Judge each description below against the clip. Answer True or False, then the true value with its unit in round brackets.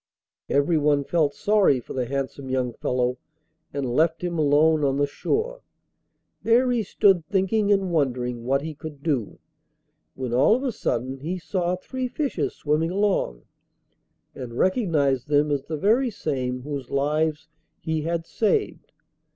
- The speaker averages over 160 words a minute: False (150 wpm)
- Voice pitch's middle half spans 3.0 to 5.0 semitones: False (5.5 semitones)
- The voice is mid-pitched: True (150 Hz)